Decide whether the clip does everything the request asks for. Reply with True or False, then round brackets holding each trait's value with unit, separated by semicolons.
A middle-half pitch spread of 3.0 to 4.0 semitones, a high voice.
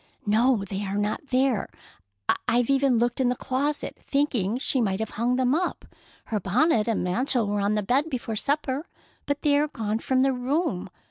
False (4.5 semitones; 245 Hz)